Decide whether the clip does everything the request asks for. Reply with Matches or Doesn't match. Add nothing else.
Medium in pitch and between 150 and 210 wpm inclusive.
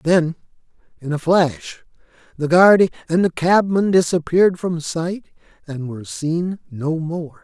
Doesn't match